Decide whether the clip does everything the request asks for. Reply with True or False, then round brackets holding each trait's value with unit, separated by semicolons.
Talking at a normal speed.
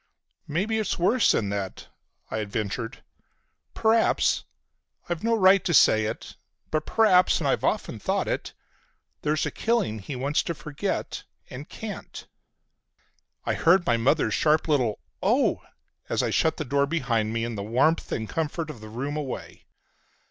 True (150 wpm)